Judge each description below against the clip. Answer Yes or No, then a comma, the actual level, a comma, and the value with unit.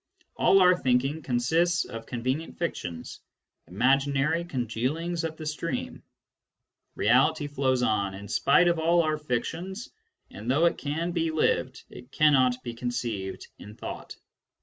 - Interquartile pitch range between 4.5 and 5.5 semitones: Yes, average, 5.0 semitones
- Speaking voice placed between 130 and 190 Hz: Yes, medium, 140 Hz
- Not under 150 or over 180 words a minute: No, slow, 135 wpm